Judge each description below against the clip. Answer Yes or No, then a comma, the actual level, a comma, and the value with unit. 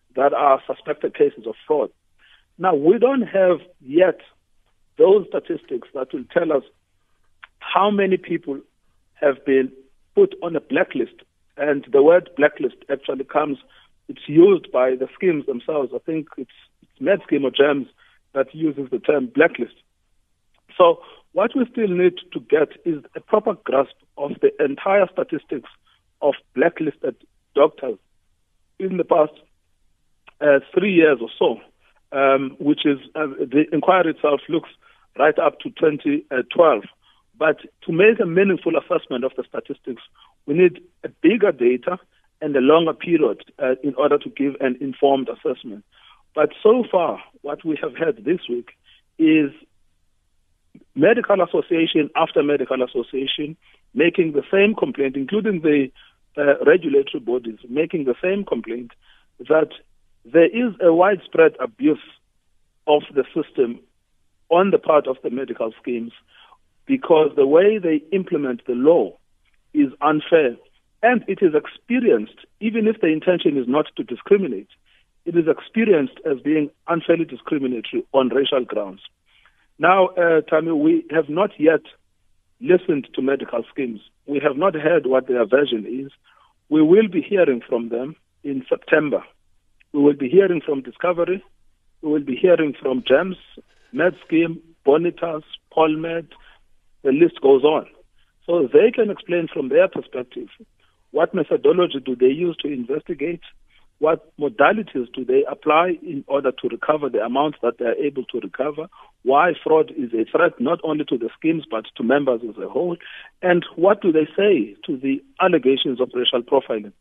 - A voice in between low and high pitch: Yes, medium, 170 Hz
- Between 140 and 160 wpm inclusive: Yes, average, 150 wpm